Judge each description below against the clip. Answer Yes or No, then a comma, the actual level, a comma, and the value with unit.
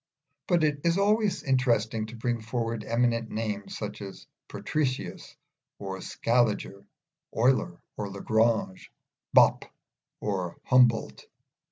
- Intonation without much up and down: No, average, 3.5 semitones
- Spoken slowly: Yes, slow, 110 wpm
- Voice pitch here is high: No, low, 115 Hz